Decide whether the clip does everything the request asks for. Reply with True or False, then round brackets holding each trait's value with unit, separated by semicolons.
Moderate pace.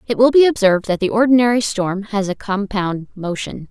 True (195 wpm)